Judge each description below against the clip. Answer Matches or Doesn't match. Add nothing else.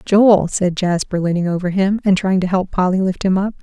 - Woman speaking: Matches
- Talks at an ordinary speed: Doesn't match